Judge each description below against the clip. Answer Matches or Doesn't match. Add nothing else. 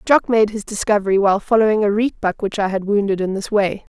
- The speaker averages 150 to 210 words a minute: Doesn't match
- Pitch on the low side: Doesn't match